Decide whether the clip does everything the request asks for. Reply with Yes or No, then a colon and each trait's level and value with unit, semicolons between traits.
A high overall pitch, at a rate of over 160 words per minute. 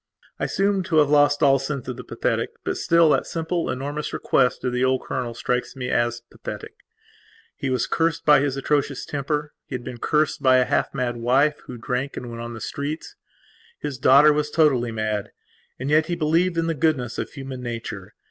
No: low, 135 Hz; average, 200 wpm